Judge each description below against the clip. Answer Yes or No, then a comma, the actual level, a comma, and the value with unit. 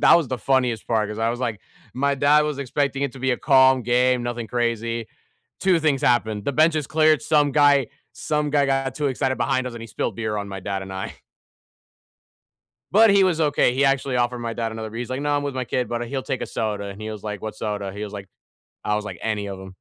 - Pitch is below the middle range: Yes, low, 125 Hz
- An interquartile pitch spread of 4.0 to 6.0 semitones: Yes, average, 4.3 semitones